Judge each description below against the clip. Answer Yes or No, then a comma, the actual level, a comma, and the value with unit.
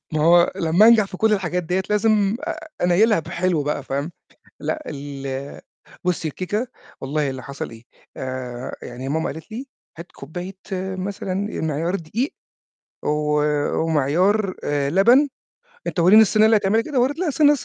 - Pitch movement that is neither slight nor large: No, wide, 6.5 semitones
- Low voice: No, medium, 180 Hz